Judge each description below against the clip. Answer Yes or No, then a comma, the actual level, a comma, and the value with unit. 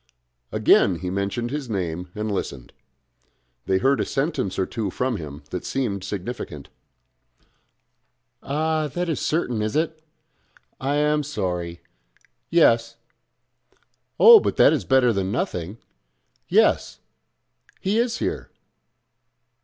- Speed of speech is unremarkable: No, slow, 120 wpm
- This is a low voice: Yes, low, 115 Hz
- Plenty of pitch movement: Yes, wide, 7.8 semitones